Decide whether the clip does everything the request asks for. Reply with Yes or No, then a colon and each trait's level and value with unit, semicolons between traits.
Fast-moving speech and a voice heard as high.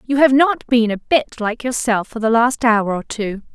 Yes: fast, 235 wpm; high, 235 Hz